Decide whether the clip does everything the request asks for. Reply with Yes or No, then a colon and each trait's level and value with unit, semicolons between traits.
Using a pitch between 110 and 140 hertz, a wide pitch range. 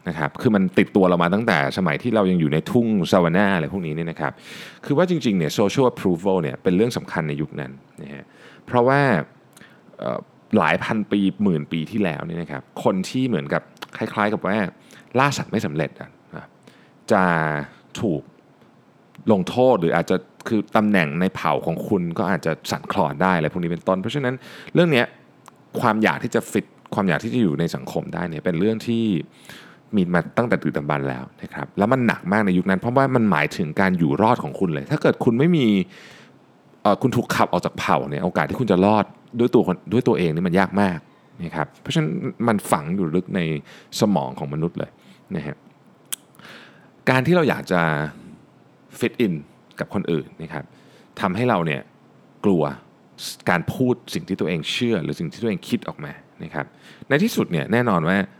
No: very low, 95 Hz; wide, 6.7 semitones